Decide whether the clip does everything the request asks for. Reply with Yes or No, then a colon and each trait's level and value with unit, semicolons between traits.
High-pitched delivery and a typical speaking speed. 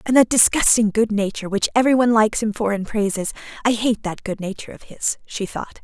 No: high, 220 Hz; fast, 215 wpm